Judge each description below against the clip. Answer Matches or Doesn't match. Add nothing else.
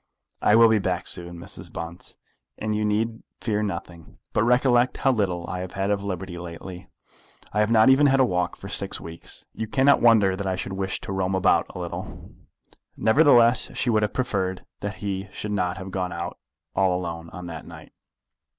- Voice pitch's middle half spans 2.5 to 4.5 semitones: Matches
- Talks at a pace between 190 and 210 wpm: Matches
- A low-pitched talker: Matches